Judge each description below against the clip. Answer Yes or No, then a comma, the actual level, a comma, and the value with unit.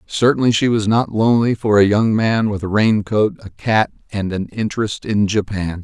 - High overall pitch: No, low, 105 Hz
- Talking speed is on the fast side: No, average, 195 wpm